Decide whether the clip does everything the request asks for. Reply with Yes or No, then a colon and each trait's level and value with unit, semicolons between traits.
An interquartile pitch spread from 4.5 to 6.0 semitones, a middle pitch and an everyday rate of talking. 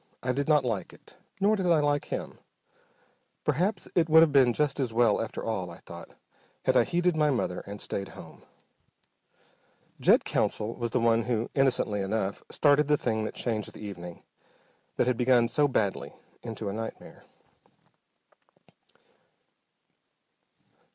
No: wide, 5.4 semitones; low, 120 Hz; average, 150 wpm